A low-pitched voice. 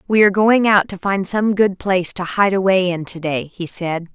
No: high, 190 Hz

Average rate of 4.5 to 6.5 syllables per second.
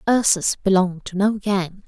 Yes: 5.0 syllables/s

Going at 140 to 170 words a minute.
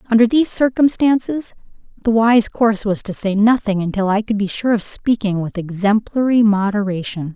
Yes: average, 165 wpm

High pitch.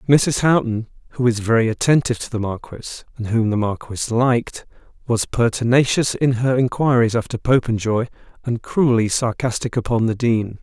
No: low, 120 Hz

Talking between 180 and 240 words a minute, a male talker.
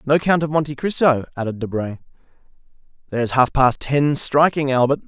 No: average, 165 wpm; male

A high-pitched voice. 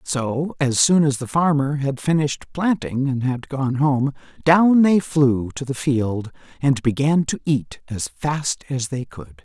No: medium, 140 Hz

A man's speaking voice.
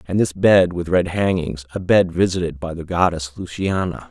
Yes: male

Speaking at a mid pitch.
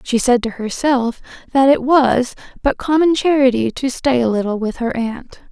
No: very high, 250 Hz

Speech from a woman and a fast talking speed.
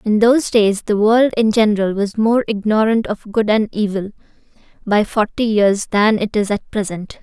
No: female; average, 185 wpm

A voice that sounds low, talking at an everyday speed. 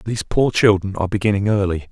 Yes: low, 100 Hz; average, 190 wpm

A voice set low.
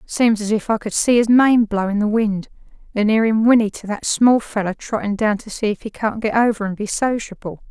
No: high, 215 Hz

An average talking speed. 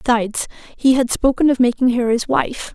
Yes: average, 195 wpm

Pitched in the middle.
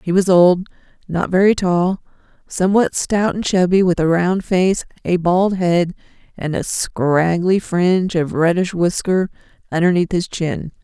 Yes: medium, 180 Hz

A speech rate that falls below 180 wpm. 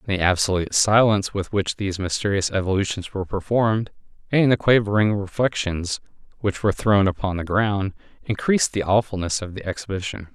Yes: average, 150 wpm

